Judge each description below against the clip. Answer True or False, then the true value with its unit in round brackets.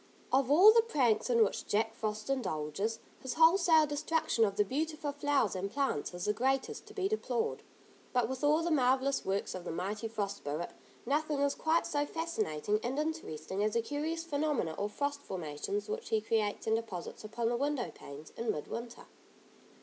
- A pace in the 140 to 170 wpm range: False (185 wpm)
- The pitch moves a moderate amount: False (6.4 semitones)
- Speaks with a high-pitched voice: True (250 Hz)